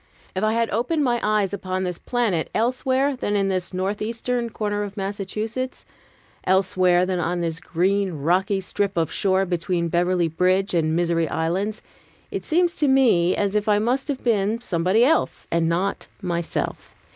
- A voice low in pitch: No, high, 195 Hz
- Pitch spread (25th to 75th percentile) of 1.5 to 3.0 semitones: No, average, 4.1 semitones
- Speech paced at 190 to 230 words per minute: No, average, 170 wpm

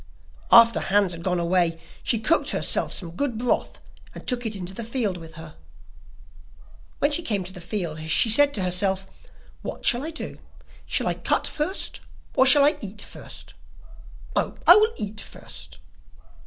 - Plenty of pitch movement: Yes, wide, 6.0 semitones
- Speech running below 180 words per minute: Yes, average, 170 wpm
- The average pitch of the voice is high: Yes, high, 205 Hz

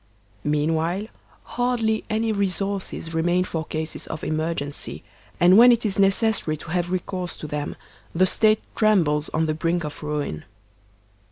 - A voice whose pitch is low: No, medium, 175 Hz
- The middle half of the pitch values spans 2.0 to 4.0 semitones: No, average, 4.4 semitones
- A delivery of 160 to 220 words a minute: No, average, 145 wpm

